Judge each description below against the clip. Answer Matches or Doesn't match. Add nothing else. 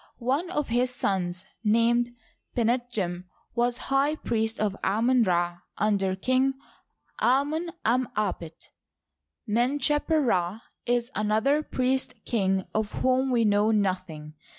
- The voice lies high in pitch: Matches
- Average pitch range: Matches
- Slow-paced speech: Matches